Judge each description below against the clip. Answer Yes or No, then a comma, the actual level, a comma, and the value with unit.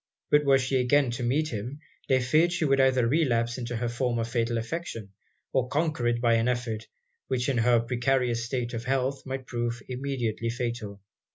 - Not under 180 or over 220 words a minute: Yes, average, 185 wpm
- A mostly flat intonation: Yes, narrow, 2.3 semitones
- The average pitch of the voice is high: No, low, 125 Hz